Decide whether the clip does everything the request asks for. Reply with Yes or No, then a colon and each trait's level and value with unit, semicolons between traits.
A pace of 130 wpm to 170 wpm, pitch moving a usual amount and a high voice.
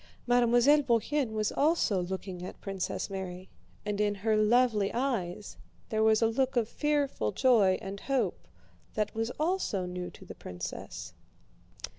Yes: average, 145 wpm; average, 4.6 semitones; high, 220 Hz